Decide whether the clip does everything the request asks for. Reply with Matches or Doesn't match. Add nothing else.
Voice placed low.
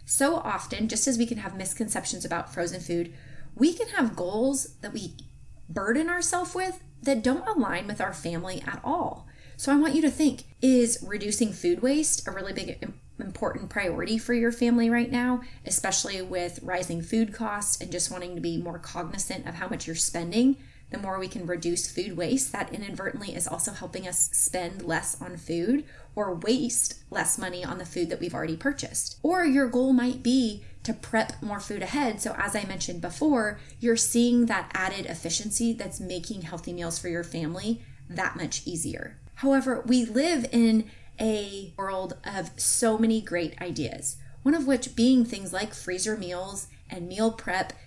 Doesn't match